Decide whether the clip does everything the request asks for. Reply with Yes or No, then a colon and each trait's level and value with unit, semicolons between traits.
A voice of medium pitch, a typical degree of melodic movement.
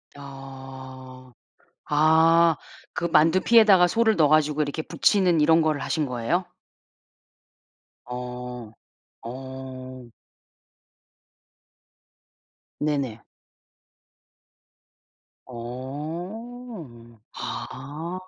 Yes: medium, 145 Hz; average, 4.5 semitones